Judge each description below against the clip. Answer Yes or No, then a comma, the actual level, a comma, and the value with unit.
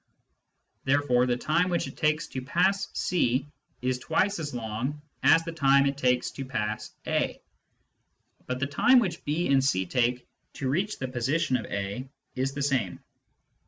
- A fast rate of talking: No, average, 165 wpm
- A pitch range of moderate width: Yes, average, 4.0 semitones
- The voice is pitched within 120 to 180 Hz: Yes, low, 135 Hz